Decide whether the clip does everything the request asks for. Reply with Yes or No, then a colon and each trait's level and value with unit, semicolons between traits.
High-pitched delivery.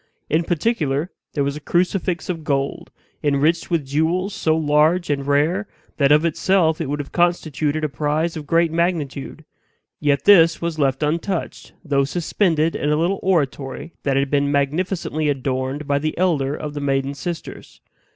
No: medium, 155 Hz